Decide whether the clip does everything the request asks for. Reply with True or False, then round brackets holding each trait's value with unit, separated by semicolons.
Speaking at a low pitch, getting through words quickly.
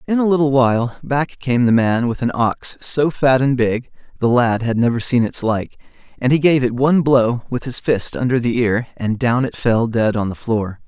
True (125 Hz; 230 wpm)